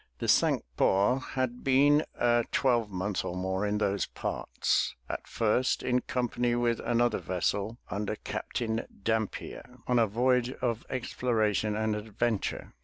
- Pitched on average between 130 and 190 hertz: No, low, 115 Hz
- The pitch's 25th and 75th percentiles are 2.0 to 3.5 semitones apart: Yes, average, 2.9 semitones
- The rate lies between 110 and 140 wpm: Yes, slow, 135 wpm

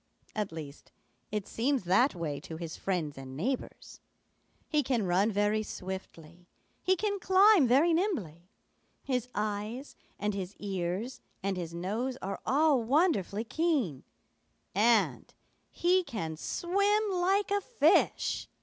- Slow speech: Yes, slow, 130 wpm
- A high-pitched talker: Yes, high, 215 Hz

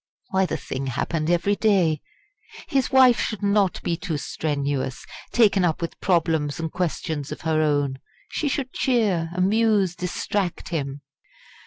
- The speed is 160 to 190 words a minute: No, average, 145 wpm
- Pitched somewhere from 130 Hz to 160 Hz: No, medium, 175 Hz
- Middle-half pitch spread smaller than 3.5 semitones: No, average, 4.8 semitones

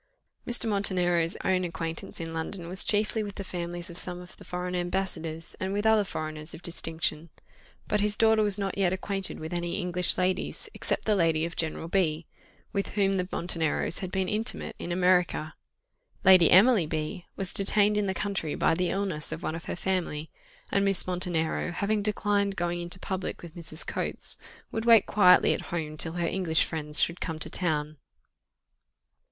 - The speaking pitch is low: No, medium, 180 Hz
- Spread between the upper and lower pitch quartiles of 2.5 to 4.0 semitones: Yes, average, 3.1 semitones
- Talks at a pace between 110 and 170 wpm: No, average, 180 wpm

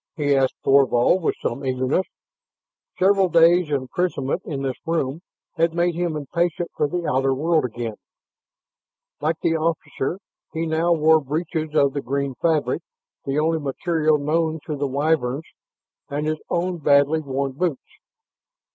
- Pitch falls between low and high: Yes, medium, 155 Hz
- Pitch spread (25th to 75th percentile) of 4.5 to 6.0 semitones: No, average, 3.2 semitones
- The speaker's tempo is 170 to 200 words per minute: No, average, 145 wpm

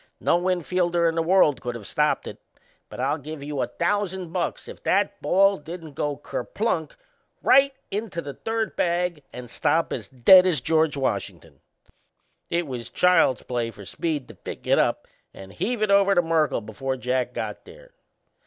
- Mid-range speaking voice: Yes, medium, 165 Hz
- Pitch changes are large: Yes, wide, 6.1 semitones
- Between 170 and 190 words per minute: Yes, average, 175 wpm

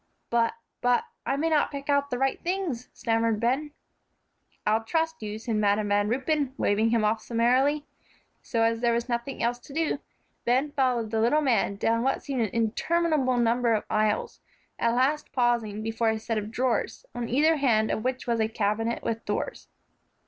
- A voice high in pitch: Yes, high, 235 Hz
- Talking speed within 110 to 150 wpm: No, average, 185 wpm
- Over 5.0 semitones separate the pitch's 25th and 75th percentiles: No, average, 3.4 semitones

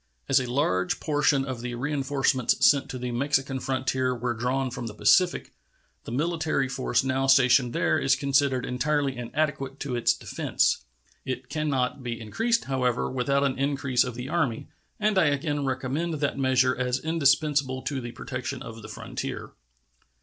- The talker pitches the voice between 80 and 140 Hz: Yes, low, 135 Hz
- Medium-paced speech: Yes, average, 165 wpm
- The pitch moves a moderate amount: No, narrow, 2.3 semitones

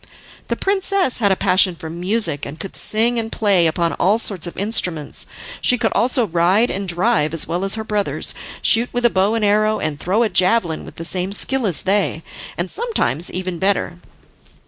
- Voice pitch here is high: Yes, high, 195 Hz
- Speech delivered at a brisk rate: No, average, 195 wpm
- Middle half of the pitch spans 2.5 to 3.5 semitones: No, average, 4.4 semitones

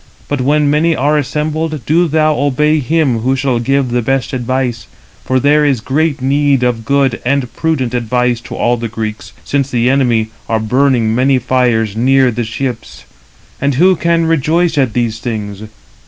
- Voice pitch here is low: Yes, low, 130 Hz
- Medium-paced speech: Yes, average, 170 wpm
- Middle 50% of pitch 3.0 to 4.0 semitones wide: Yes, average, 3.6 semitones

